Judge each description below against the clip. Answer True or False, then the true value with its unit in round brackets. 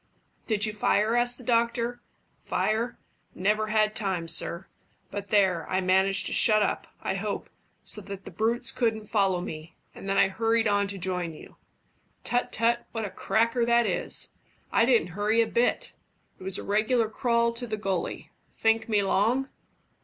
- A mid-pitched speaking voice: False (215 Hz)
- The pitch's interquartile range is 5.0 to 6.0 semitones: False (3.1 semitones)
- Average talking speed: True (175 wpm)